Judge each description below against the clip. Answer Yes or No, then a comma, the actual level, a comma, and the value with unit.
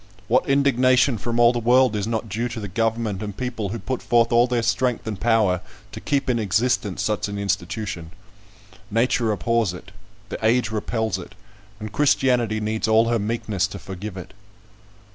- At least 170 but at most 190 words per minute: Yes, average, 180 wpm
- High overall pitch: No, low, 110 Hz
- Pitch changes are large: No, average, 2.7 semitones